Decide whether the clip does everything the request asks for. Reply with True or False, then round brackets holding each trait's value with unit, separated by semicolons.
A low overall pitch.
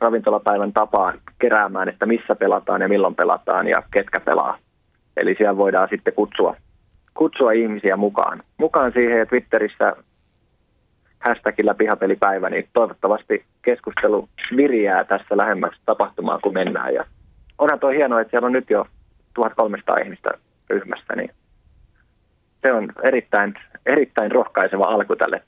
True (110 Hz)